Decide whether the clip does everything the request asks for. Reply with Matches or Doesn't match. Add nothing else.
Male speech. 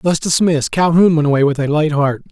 Matches